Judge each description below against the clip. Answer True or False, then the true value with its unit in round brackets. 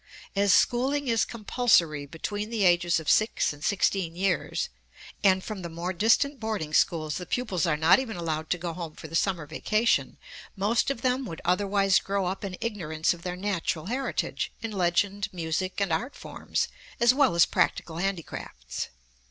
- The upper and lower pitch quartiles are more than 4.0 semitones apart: True (4.5 semitones)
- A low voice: False (190 Hz)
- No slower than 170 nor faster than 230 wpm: True (175 wpm)